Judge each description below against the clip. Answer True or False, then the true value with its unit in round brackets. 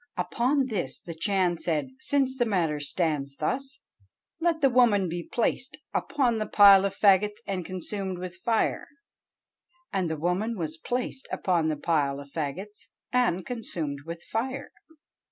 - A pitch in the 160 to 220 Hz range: True (190 Hz)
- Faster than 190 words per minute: False (150 wpm)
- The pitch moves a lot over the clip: True (6.2 semitones)